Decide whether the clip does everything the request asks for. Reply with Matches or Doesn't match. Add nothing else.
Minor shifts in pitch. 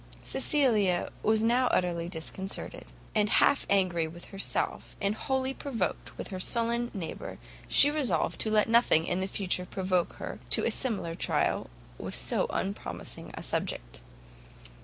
Doesn't match